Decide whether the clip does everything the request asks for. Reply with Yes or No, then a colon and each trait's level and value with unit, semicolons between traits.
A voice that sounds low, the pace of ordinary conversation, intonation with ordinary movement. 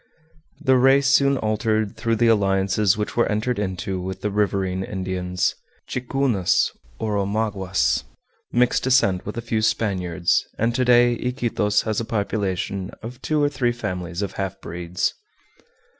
Yes: low, 105 Hz; average, 145 wpm; average, 4.0 semitones